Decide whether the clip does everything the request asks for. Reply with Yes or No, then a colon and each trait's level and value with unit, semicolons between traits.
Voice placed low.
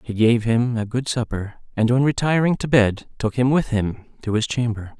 Yes: low, 120 Hz